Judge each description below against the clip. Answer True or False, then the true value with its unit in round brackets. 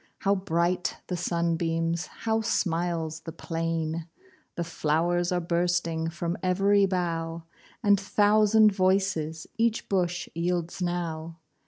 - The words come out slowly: True (115 wpm)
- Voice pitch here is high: False (175 Hz)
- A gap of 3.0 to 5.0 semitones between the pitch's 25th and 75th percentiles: False (2.5 semitones)